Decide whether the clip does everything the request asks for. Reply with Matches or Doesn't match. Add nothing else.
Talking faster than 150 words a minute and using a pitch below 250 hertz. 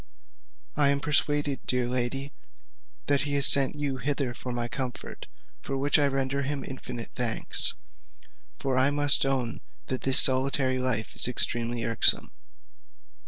Doesn't match